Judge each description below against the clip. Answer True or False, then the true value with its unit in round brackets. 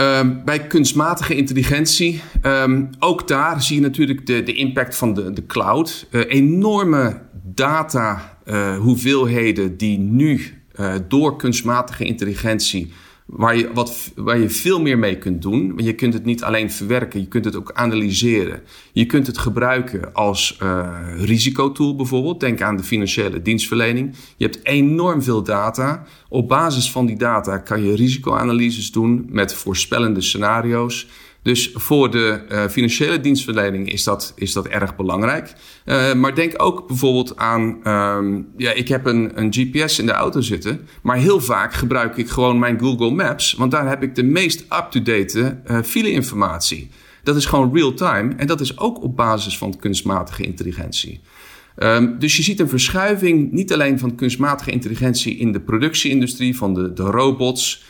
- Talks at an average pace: True (165 wpm)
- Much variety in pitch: False (4.0 semitones)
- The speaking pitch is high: False (120 Hz)